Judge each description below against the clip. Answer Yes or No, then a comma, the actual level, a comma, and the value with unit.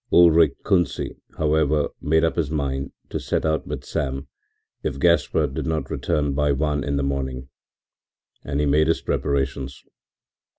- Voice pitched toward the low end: Yes, very low, 75 Hz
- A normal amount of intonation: No, narrow, 2.2 semitones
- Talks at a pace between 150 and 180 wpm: Yes, average, 155 wpm